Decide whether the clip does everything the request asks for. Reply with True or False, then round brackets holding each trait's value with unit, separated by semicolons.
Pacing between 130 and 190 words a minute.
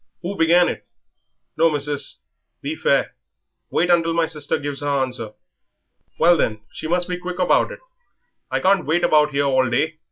True (170 wpm)